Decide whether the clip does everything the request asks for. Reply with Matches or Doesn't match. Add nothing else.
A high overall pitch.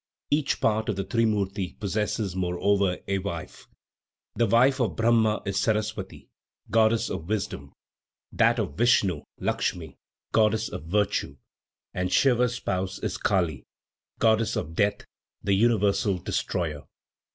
Doesn't match